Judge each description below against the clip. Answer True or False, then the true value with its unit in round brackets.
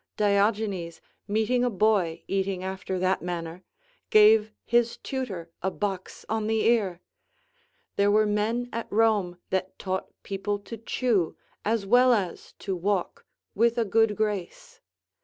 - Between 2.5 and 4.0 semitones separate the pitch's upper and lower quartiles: True (2.9 semitones)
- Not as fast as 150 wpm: True (140 wpm)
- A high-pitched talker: True (205 Hz)